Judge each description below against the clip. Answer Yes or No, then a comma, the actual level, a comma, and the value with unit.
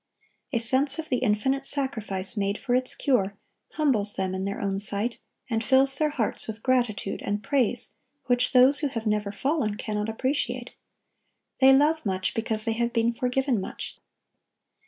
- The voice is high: Yes, high, 235 Hz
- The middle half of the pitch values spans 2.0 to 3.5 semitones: No, average, 4.3 semitones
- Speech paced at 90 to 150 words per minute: No, average, 165 wpm